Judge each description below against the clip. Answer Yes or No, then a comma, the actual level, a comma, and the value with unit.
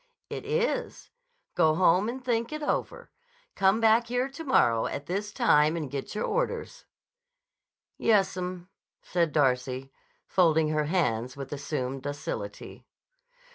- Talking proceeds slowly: Yes, slow, 130 wpm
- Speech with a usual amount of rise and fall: No, wide, 8.4 semitones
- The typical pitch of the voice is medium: Yes, medium, 180 Hz